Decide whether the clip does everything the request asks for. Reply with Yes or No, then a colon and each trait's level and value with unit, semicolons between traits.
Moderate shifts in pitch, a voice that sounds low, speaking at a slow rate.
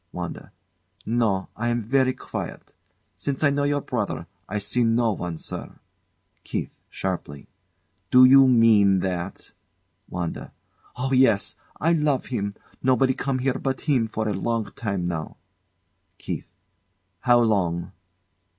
Yes: average, 5.0 semitones; low, 115 Hz; slow, 130 wpm